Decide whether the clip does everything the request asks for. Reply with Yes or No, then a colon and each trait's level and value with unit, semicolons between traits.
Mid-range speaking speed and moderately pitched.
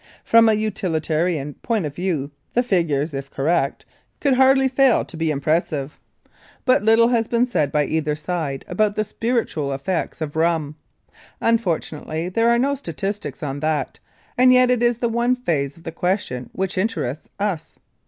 Yes: average, 165 wpm; medium, 175 Hz